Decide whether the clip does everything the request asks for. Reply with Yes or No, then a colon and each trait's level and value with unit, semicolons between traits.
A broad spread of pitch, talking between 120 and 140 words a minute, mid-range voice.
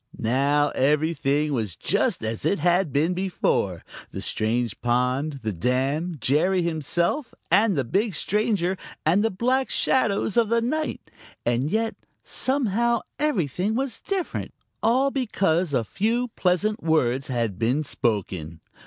Yes: wide, 9.0 semitones; slow, 135 wpm; medium, 170 Hz